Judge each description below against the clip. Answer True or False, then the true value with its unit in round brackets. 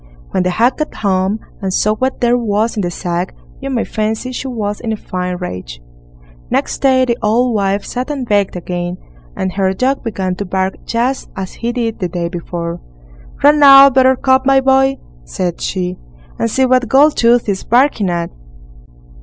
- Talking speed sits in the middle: True (180 wpm)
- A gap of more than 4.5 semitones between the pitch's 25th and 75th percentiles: True (5.6 semitones)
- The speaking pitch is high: True (220 Hz)